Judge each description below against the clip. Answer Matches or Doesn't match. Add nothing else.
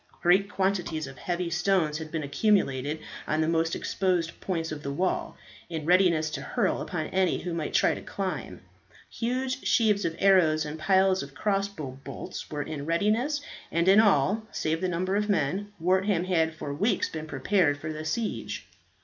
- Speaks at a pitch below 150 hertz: Doesn't match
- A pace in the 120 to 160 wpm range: Doesn't match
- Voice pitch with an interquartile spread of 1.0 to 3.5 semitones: Doesn't match